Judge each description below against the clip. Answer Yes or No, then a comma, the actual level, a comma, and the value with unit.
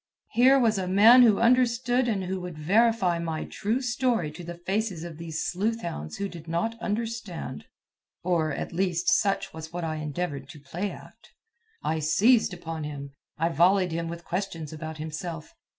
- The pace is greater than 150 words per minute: Yes, average, 175 wpm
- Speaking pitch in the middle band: Yes, medium, 175 Hz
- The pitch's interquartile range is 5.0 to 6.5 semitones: Yes, average, 5.3 semitones